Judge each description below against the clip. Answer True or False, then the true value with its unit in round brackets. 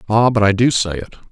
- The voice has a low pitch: True (110 Hz)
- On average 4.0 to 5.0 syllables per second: False (6.1 syllables/s)